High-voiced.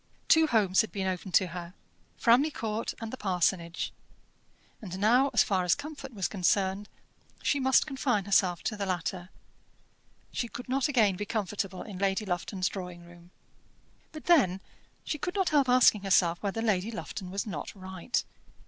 Yes: high, 200 Hz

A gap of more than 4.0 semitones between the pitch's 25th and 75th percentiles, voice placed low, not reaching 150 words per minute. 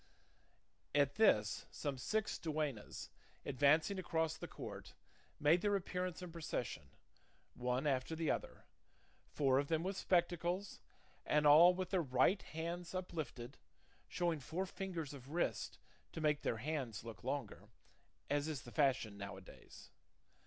No: average, 5.0 semitones; medium, 155 Hz; average, 140 wpm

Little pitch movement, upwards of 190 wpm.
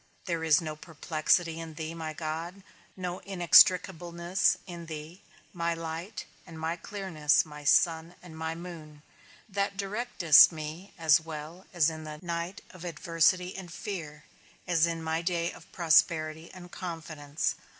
No: narrow, 2.1 semitones; average, 140 wpm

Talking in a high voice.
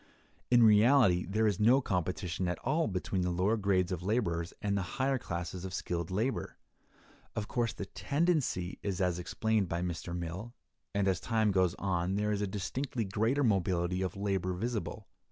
No: low, 100 Hz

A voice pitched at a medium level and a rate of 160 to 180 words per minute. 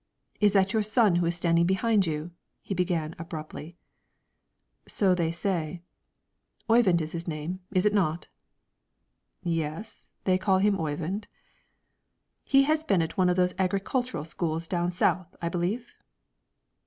No: medium, 180 Hz; average, 140 wpm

